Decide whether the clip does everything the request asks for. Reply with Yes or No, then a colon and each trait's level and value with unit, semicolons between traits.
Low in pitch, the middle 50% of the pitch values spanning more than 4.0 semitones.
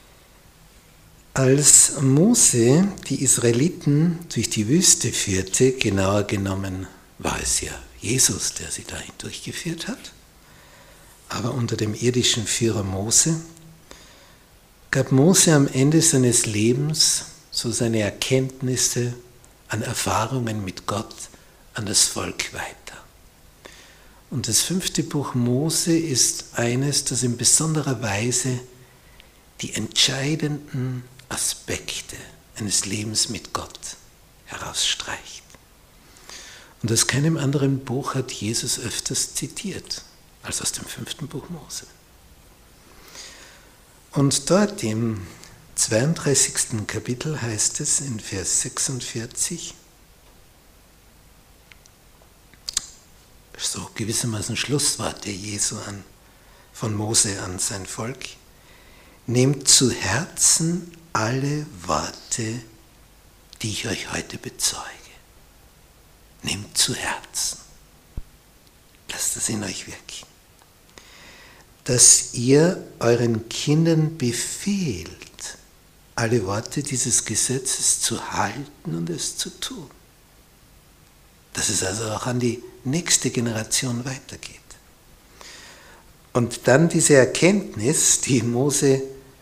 Yes: low, 125 Hz; average, 4.4 semitones